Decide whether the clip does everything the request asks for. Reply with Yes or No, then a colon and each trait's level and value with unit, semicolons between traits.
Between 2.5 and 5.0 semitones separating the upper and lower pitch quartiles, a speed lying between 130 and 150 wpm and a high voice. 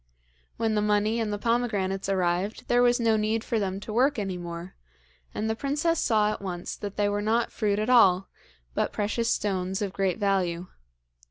No: average, 2.9 semitones; average, 190 wpm; high, 210 Hz